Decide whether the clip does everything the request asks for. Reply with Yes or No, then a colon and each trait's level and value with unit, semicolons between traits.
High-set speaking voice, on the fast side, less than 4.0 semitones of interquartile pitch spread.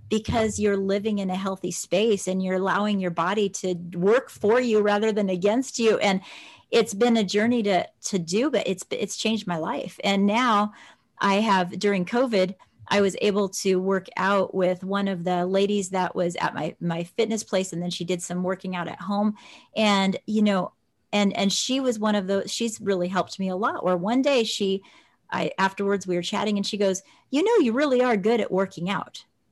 Yes: high, 200 Hz; fast, 210 wpm; narrow, 2.5 semitones